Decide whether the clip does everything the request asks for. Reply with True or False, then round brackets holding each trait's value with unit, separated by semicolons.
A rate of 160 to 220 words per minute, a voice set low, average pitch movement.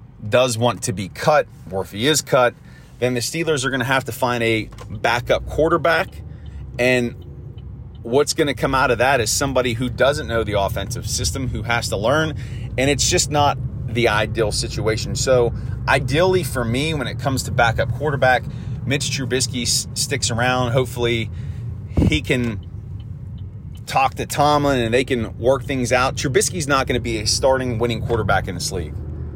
True (175 wpm; 120 Hz; 3.0 semitones)